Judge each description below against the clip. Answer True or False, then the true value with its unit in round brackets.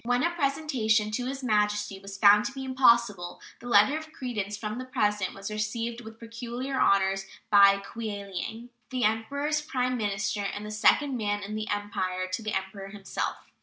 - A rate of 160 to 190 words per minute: True (175 wpm)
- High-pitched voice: True (215 Hz)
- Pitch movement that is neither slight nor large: True (3.5 semitones)